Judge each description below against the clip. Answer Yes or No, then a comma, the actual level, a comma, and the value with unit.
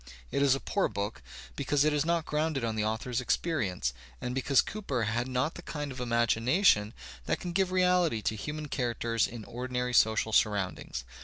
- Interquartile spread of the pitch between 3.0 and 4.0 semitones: No, average, 5.3 semitones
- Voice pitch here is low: Yes, low, 125 Hz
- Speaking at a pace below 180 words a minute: No, average, 185 wpm